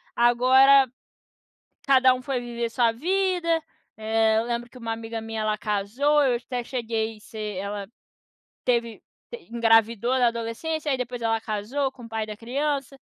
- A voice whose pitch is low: No, high, 235 Hz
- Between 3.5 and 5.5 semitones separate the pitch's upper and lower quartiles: No, average, 2.8 semitones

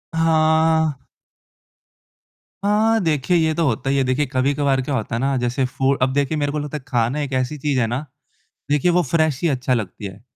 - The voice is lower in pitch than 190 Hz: Yes, medium, 140 Hz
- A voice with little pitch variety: No, average, 3.5 semitones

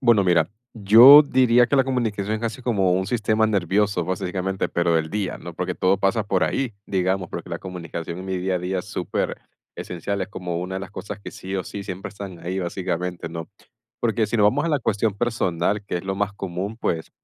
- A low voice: Yes, very low, 95 Hz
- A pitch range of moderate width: Yes, average, 3.3 semitones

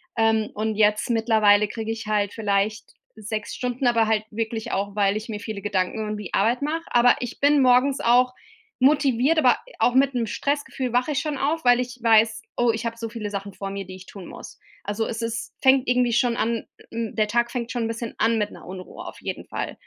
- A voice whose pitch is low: No, high, 230 Hz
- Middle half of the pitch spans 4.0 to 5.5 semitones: No, average, 2.7 semitones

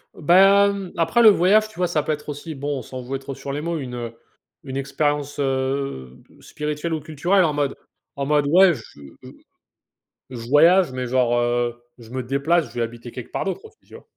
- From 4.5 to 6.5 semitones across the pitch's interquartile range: Yes, average, 4.8 semitones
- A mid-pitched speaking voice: Yes, medium, 145 Hz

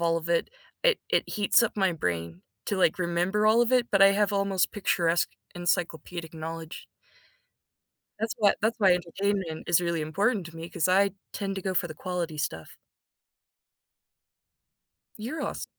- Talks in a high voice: No, medium, 180 Hz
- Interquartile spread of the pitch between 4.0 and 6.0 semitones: No, average, 3.4 semitones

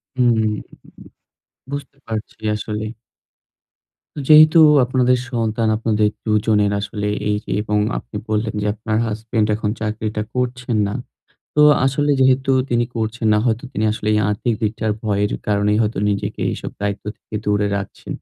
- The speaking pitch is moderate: No, low, 110 Hz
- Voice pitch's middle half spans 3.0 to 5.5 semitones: No, narrow, 2.4 semitones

